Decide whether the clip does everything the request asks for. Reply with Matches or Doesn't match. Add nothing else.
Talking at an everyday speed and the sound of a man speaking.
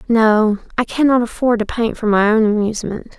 Doesn't match